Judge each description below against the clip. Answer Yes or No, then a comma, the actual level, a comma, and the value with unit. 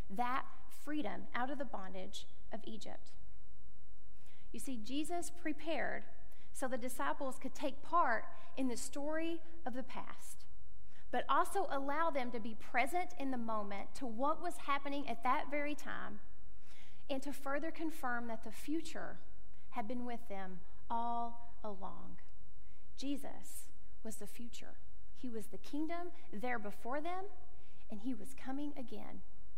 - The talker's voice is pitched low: No, very high, 260 Hz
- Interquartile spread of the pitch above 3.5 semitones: Yes, average, 5.1 semitones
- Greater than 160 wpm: No, average, 145 wpm